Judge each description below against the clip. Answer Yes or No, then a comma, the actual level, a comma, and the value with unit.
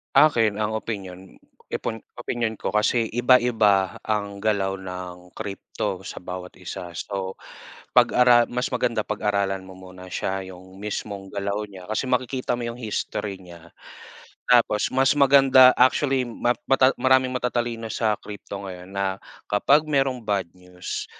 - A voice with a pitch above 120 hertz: No, low, 105 Hz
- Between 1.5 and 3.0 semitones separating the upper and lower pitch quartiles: No, average, 4.4 semitones